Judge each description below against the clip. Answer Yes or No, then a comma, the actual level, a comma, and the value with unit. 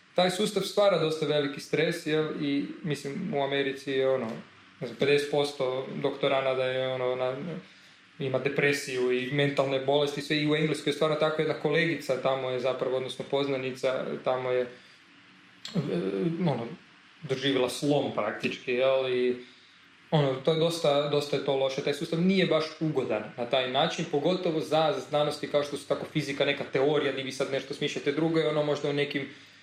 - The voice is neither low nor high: Yes, medium, 145 Hz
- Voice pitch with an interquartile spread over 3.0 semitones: No, narrow, 2.6 semitones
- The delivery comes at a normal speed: No, fast, 170 wpm